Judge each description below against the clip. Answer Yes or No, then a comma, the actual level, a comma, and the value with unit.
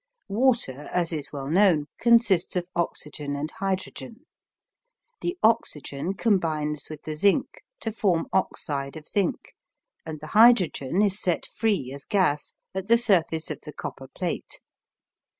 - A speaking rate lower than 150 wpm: Yes, average, 140 wpm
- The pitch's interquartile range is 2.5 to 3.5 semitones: No, average, 5.3 semitones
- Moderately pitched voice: Yes, medium, 175 Hz